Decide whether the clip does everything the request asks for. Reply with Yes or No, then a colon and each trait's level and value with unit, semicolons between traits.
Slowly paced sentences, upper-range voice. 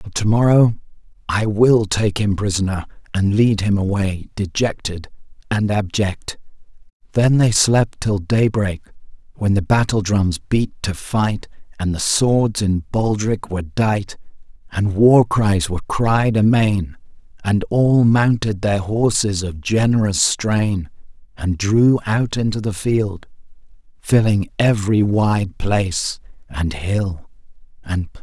No: slow, 130 wpm; low, 105 Hz